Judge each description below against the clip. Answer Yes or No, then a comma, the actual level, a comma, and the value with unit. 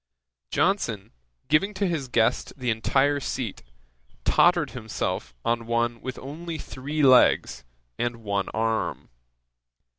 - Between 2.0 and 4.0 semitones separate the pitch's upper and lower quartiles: No, average, 4.9 semitones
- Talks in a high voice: No, low, 125 Hz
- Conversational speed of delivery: No, slow, 115 wpm